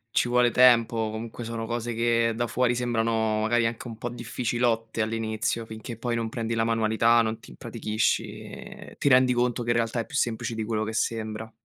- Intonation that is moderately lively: No, narrow, 1.2 semitones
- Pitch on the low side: Yes, low, 115 Hz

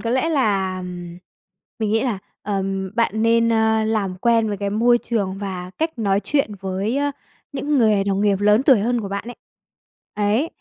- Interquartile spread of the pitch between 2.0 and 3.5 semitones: Yes, average, 3.0 semitones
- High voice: Yes, high, 215 Hz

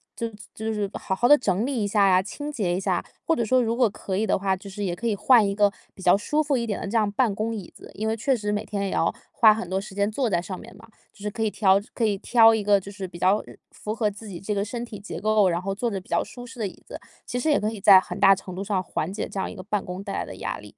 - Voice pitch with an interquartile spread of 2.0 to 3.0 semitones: Yes, average, 2.7 semitones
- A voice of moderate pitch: No, high, 205 Hz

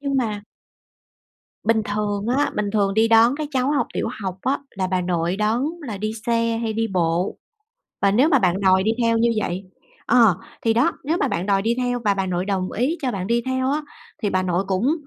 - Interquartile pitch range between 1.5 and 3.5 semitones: No, average, 4.3 semitones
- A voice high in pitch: Yes, high, 215 Hz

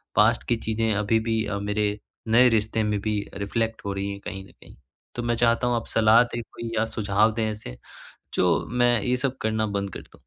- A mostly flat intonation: Yes, narrow, 2.1 semitones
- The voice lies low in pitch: Yes, low, 110 Hz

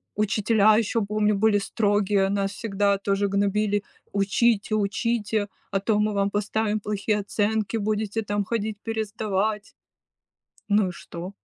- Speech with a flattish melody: Yes, narrow, 1.4 semitones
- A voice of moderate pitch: No, high, 205 Hz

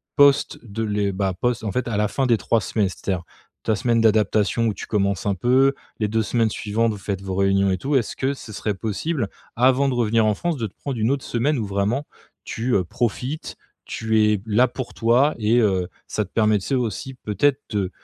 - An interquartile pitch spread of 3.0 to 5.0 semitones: Yes, average, 3.6 semitones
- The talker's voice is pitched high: No, low, 110 Hz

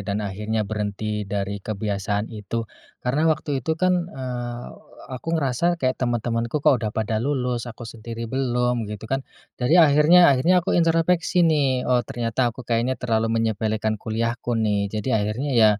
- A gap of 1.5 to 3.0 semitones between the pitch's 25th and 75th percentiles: No, average, 3.8 semitones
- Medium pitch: No, low, 120 Hz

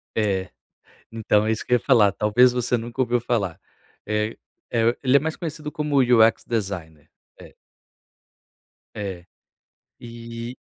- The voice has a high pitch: No, low, 115 Hz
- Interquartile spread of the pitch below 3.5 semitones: Yes, average, 2.9 semitones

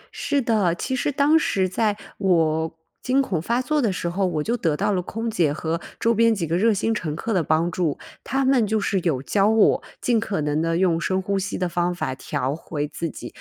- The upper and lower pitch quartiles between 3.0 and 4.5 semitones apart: No, wide, 5.4 semitones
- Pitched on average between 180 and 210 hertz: Yes, medium, 185 Hz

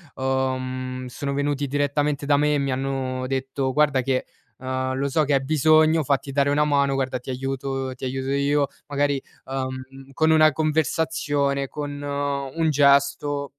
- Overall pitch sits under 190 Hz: Yes, medium, 140 Hz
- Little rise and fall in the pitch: Yes, narrow, 1.6 semitones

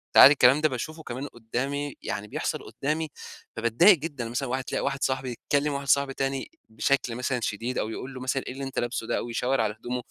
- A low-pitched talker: Yes, low, 130 Hz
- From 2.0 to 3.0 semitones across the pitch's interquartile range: Yes, average, 2.7 semitones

